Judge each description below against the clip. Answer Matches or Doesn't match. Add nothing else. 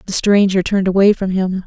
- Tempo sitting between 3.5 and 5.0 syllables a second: Doesn't match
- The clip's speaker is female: Matches